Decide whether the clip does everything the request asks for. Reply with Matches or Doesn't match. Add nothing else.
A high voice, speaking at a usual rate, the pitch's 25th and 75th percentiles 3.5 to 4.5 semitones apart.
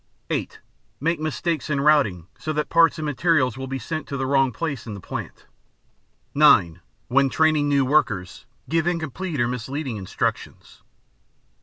Doesn't match